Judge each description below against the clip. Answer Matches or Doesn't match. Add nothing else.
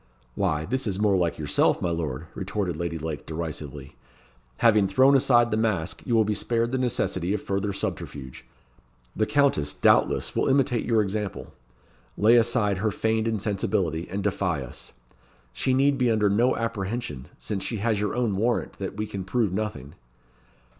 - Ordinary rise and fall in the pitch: Matches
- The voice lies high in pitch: Doesn't match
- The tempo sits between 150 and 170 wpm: Matches